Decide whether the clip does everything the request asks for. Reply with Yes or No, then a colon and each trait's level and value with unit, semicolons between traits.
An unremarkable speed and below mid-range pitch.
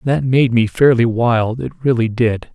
Yes: average, 190 wpm; low, 120 Hz